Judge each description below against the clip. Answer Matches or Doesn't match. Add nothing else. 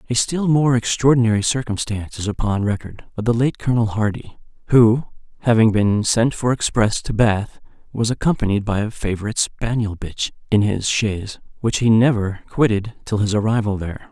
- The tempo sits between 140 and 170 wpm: Matches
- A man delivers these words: Matches